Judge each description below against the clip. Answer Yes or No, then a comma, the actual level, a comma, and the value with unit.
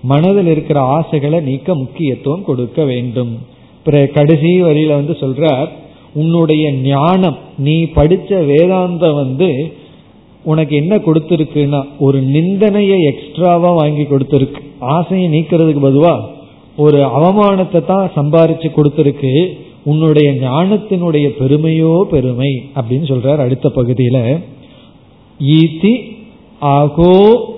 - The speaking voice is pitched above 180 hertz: No, medium, 155 Hz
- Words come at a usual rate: Yes, average, 95 wpm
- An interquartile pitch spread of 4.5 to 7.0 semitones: No, average, 3.4 semitones